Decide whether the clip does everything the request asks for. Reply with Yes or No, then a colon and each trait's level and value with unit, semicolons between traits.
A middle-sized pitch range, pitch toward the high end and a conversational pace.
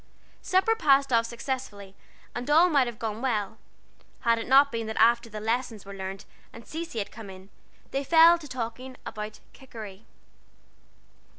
Yes: average, 4.1 semitones; high, 235 Hz; average, 165 wpm